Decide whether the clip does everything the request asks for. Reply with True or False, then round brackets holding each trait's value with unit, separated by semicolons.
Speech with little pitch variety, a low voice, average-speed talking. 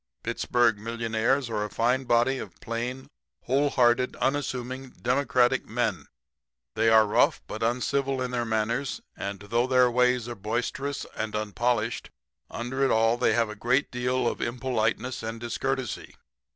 True (2.2 semitones; 120 Hz; 145 wpm)